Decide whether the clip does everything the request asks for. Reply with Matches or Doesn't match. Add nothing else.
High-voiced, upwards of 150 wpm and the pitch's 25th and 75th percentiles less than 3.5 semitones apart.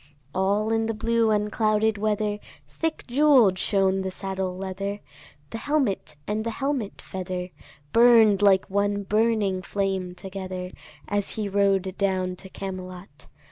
Doesn't match